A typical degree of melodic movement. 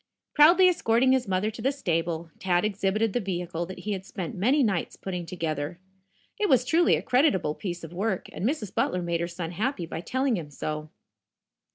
No: wide, 6.1 semitones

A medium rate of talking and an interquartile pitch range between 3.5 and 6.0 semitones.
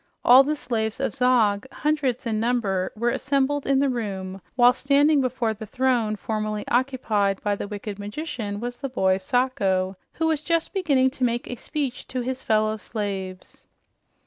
Yes: average, 170 wpm; average, 4.1 semitones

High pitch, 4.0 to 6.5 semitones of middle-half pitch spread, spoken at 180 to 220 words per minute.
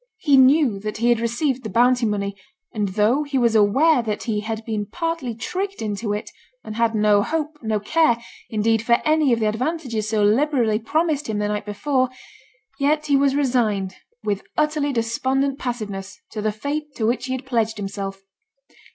Yes: high, 235 Hz; average, 4.8 semitones; average, 185 wpm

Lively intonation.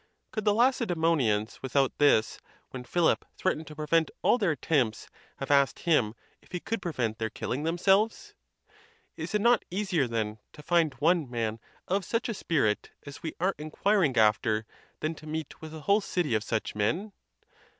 Yes: wide, 6.8 semitones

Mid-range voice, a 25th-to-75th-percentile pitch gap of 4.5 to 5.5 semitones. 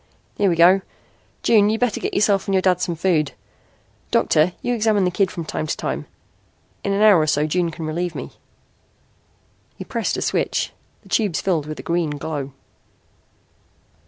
No: medium, 175 Hz; average, 4.1 semitones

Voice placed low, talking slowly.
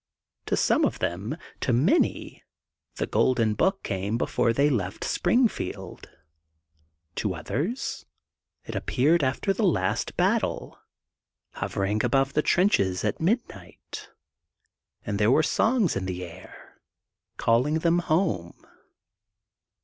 Yes: low, 130 Hz; slow, 115 wpm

